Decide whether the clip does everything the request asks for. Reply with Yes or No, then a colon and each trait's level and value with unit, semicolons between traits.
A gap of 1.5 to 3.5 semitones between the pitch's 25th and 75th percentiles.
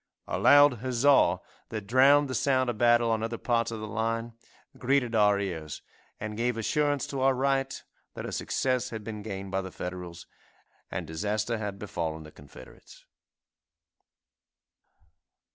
No: average, 4.6 semitones